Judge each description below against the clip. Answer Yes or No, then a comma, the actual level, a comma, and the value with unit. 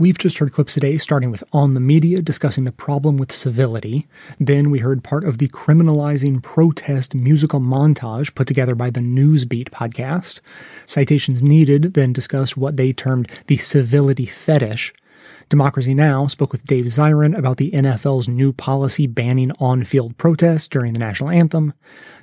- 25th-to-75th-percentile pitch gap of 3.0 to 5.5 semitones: No, narrow, 2.4 semitones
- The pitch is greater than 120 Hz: Yes, medium, 140 Hz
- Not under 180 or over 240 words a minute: No, average, 160 wpm